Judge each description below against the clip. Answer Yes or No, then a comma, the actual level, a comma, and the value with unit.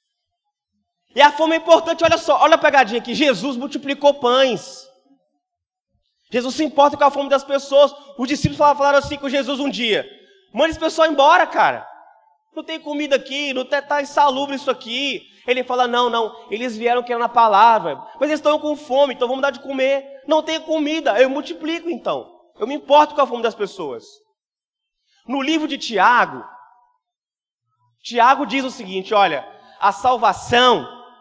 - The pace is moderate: Yes, average, 170 wpm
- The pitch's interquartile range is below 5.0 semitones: Yes, average, 3.7 semitones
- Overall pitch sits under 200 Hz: No, very high, 280 Hz